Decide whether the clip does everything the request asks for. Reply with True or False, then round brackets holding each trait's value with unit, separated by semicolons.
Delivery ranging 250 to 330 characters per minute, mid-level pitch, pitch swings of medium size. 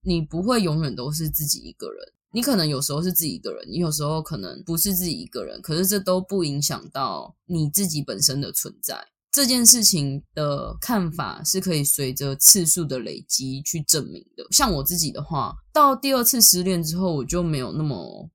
True (305 characters per minute; 170 Hz; 4.7 semitones)